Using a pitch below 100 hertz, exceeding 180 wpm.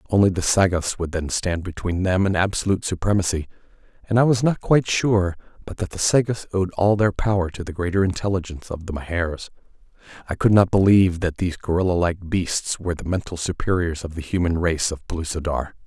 Yes: very low, 90 Hz; average, 190 wpm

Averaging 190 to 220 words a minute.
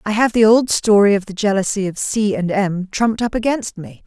Yes: fast, 205 wpm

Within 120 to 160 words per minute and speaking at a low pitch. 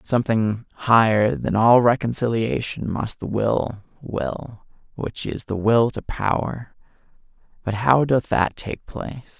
Yes: slow, 135 wpm; low, 115 Hz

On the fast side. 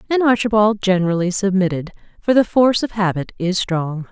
No: average, 160 wpm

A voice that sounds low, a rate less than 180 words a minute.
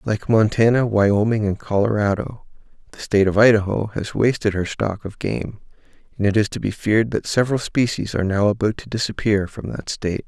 No: low, 105 Hz; average, 185 wpm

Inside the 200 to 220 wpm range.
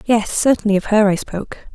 Yes: fast, 205 wpm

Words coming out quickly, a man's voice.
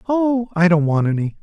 Yes: fast, 210 wpm; male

